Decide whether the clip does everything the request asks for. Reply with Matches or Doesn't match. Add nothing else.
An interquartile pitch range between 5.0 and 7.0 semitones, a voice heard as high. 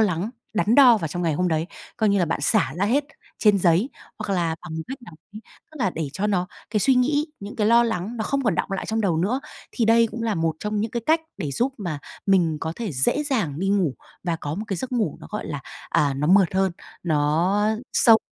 Matches